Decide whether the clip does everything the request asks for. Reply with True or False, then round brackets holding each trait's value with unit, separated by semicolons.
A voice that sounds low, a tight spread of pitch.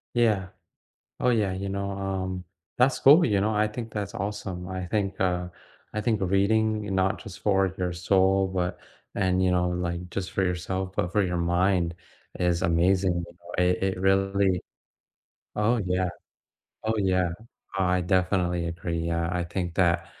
True (95 Hz; 1.9 semitones)